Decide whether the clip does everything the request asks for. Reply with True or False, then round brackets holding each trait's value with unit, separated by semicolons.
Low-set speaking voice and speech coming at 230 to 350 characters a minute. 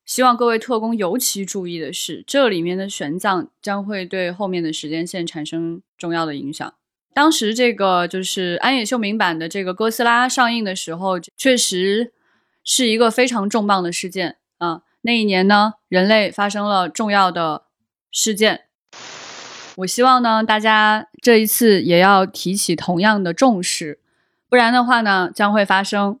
False (200 Hz; 255 characters per minute)